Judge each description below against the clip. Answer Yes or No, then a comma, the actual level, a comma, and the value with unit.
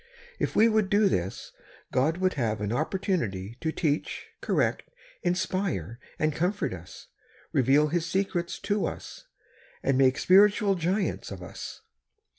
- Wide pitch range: Yes, wide, 7.1 semitones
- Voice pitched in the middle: Yes, medium, 165 Hz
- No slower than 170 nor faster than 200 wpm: No, slow, 135 wpm